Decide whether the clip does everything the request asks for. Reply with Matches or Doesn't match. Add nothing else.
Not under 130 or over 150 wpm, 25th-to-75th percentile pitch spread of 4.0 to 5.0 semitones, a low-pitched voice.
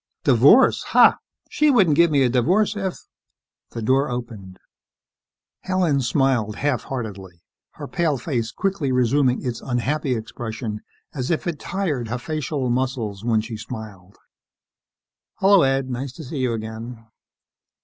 Matches